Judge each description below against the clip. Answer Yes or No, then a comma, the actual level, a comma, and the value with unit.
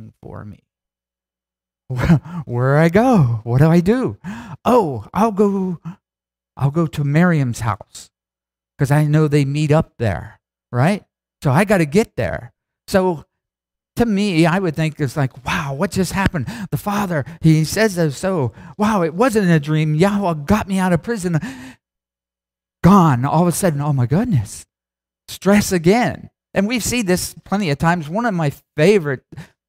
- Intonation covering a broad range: Yes, wide, 6.9 semitones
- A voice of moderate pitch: Yes, medium, 160 Hz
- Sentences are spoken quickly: No, average, 165 wpm